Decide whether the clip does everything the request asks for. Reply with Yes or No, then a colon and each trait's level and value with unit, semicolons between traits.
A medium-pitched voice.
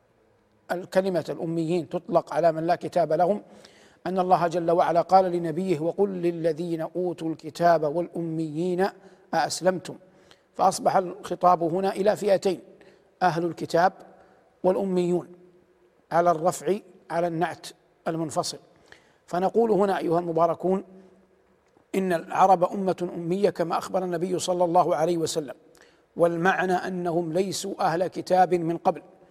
Yes: medium, 180 Hz